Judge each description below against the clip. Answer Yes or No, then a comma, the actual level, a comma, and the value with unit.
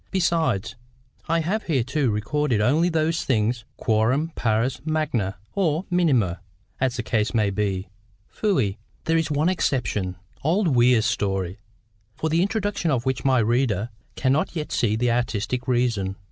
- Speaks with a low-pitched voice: Yes, low, 125 Hz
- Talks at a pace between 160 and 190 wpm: No, slow, 135 wpm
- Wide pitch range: Yes, wide, 6.6 semitones